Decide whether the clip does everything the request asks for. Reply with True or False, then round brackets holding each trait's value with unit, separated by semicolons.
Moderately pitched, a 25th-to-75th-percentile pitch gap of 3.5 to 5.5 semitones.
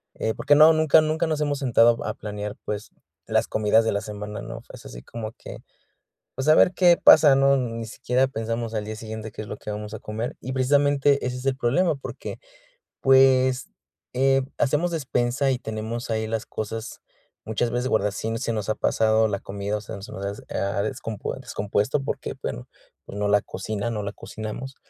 False (115 Hz; 4.0 semitones)